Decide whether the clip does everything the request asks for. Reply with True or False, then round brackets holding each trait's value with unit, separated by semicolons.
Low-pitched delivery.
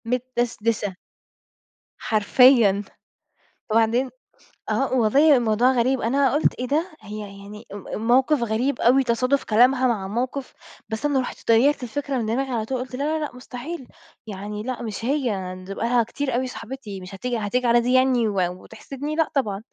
False (245 Hz)